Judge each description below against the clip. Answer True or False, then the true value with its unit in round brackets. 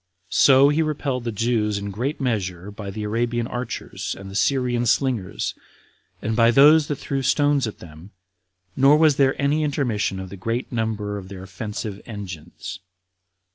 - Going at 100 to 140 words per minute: False (165 wpm)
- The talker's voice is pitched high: False (115 Hz)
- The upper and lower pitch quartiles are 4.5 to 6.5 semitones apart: True (5.1 semitones)